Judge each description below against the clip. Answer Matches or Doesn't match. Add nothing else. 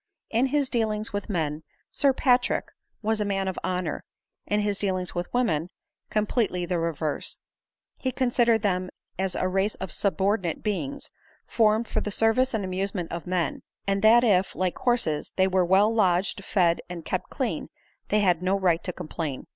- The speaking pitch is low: Doesn't match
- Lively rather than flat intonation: Doesn't match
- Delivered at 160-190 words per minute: Matches